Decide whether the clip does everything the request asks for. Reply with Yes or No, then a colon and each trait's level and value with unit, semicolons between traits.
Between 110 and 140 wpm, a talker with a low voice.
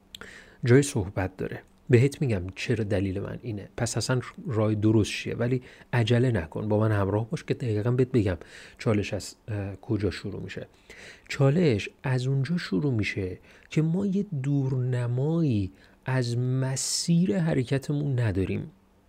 Yes: average, 135 wpm; low, 120 Hz